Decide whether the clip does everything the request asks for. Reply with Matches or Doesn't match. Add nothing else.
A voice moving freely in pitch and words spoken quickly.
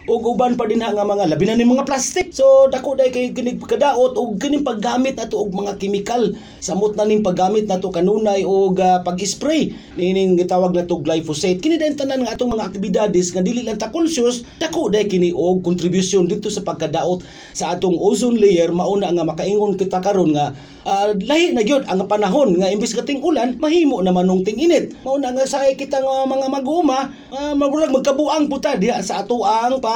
Matches